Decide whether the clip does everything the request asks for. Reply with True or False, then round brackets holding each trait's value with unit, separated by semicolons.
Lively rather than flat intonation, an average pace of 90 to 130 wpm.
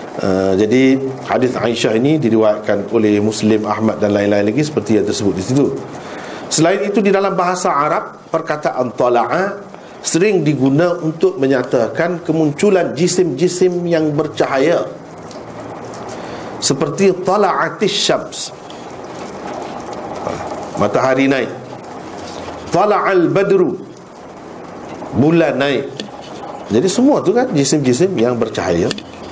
True (7.4 semitones; 100 wpm)